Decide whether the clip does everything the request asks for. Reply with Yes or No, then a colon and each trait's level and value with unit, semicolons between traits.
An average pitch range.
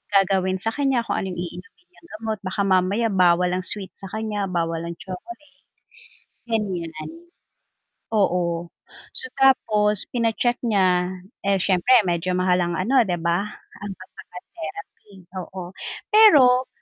Yes: average, 4.2 semitones